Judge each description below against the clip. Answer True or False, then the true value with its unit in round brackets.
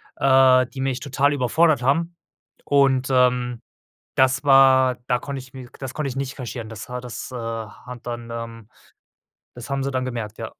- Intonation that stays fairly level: True (1.9 semitones)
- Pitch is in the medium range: False (130 Hz)